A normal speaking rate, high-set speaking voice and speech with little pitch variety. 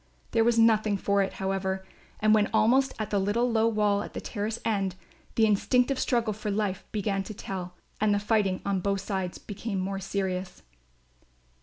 Yes: average, 180 wpm; high, 205 Hz; narrow, 2.3 semitones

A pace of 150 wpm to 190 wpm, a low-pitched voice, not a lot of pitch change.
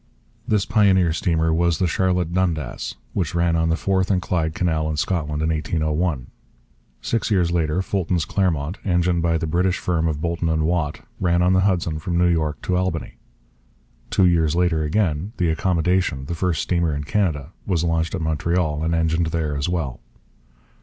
Yes: average, 180 wpm; very low, 85 Hz; narrow, 2.3 semitones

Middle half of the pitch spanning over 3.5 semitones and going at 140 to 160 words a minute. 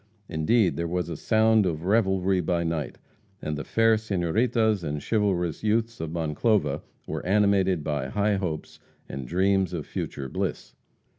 Yes: average, 4.8 semitones; average, 150 wpm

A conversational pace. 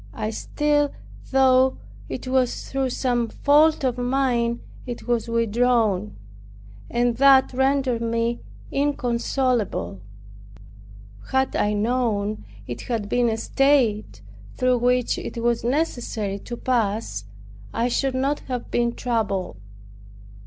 No: slow, 115 wpm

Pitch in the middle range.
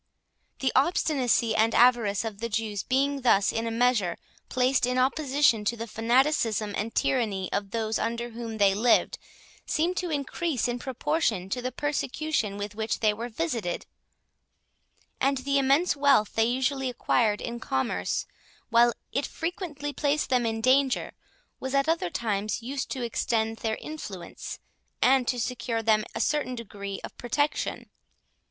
No: high, 240 Hz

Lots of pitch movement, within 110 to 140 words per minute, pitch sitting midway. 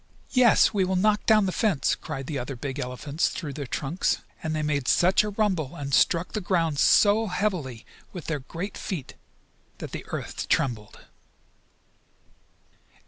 No: wide, 6.1 semitones; average, 160 wpm; medium, 165 Hz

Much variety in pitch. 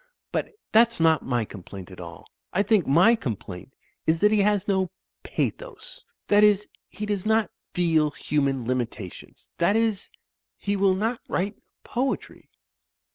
Yes: wide, 7.5 semitones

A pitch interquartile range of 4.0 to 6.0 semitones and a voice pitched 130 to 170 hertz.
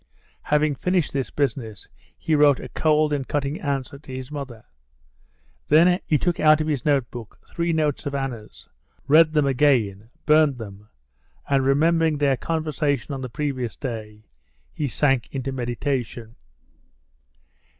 No: average, 3.5 semitones; medium, 140 Hz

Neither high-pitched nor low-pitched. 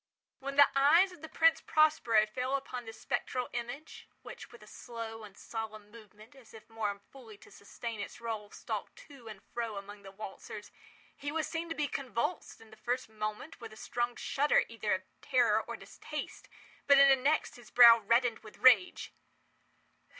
No: high, 235 Hz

